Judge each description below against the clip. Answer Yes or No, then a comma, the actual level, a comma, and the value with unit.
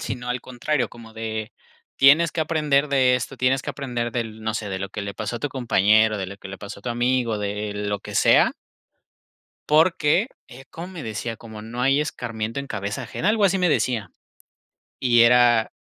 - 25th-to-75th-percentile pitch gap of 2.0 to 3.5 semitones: No, average, 4.2 semitones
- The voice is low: Yes, low, 120 Hz